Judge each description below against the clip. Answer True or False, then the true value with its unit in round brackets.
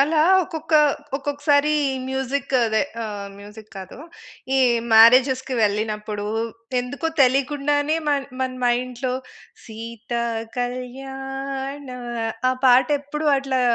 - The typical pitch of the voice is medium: False (260 Hz)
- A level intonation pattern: False (3.2 semitones)